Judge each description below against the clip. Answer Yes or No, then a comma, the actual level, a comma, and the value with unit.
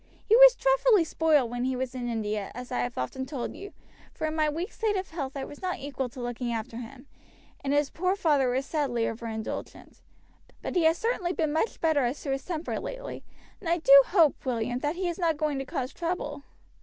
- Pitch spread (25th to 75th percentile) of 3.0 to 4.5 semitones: No, wide, 5.5 semitones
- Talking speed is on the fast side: Yes, fast, 220 wpm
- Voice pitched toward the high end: Yes, very high, 290 Hz